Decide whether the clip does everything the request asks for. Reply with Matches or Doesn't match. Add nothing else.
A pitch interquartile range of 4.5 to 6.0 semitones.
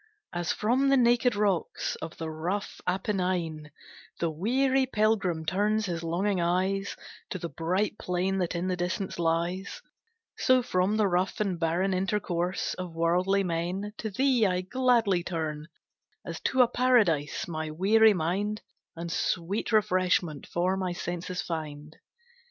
Doesn't match